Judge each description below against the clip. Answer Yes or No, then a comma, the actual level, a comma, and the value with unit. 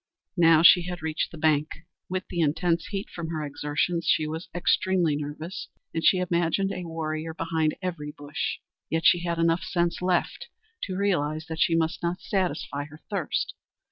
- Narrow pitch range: Yes, narrow, 2.3 semitones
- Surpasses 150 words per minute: Yes, average, 175 wpm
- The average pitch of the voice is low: No, medium, 165 Hz